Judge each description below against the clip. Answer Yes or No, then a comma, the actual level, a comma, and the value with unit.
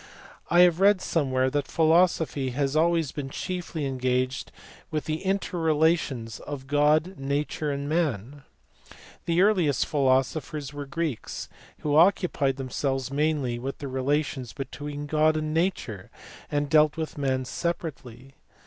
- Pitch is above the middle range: No, medium, 145 Hz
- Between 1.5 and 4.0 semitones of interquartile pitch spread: Yes, average, 3.2 semitones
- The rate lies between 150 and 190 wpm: No, slow, 135 wpm